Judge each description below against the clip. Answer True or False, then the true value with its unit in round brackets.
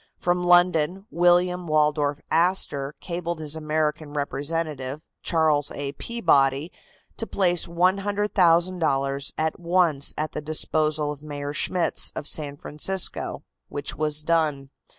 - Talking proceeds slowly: True (115 wpm)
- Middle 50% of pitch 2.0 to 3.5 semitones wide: True (3.2 semitones)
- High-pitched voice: False (155 Hz)